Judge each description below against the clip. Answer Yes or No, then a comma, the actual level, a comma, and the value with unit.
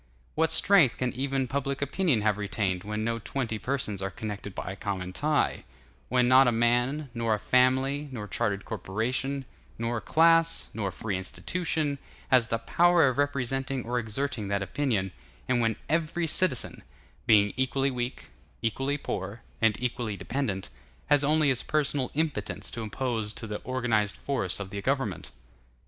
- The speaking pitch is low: Yes, low, 125 Hz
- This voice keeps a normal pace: Yes, average, 155 wpm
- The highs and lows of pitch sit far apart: No, average, 4.7 semitones